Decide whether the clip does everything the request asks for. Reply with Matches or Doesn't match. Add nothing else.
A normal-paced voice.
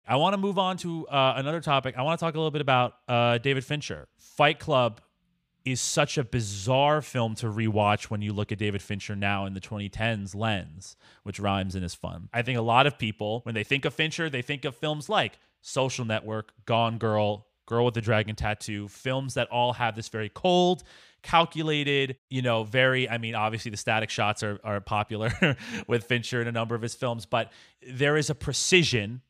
Doesn't match